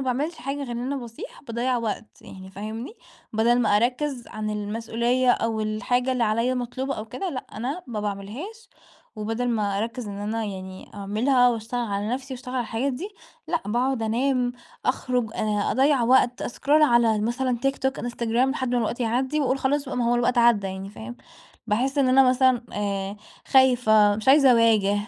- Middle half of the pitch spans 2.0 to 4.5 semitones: Yes, average, 3.2 semitones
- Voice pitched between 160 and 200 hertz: No, high, 240 Hz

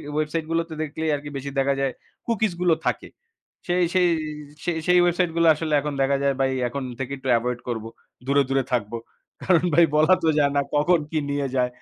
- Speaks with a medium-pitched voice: Yes, medium, 150 Hz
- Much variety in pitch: No, average, 3.7 semitones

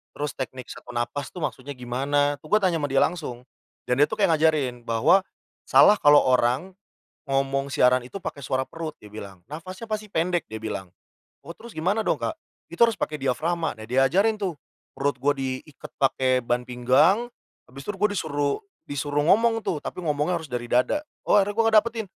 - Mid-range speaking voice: Yes, medium, 145 Hz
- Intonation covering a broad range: Yes, wide, 6.0 semitones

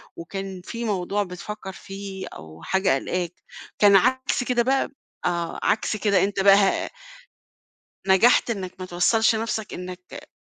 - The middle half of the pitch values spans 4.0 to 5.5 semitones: No, average, 3.2 semitones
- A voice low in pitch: No, high, 195 Hz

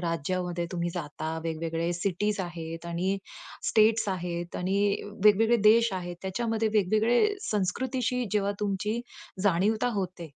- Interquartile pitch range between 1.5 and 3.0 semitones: No, average, 3.9 semitones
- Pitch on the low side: No, high, 190 Hz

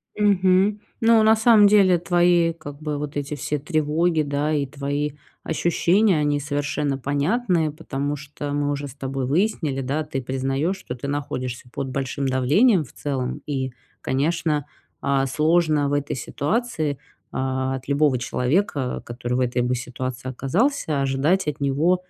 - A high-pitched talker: No, medium, 145 Hz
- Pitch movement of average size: Yes, average, 4.1 semitones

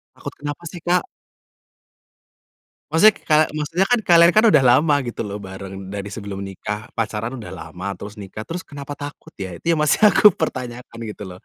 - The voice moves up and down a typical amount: No, wide, 8.3 semitones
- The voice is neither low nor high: No, low, 125 Hz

